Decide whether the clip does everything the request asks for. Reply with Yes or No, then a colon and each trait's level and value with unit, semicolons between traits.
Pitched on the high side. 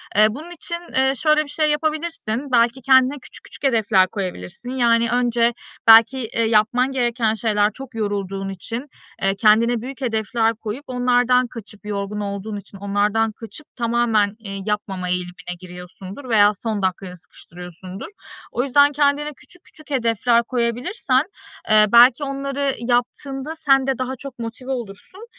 Yes: high, 235 Hz